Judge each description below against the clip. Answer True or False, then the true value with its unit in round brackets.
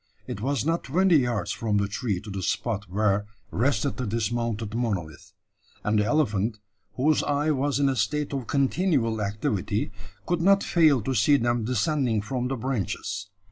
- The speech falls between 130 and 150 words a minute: False (170 wpm)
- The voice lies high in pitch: False (120 Hz)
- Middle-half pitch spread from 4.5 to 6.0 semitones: True (5.2 semitones)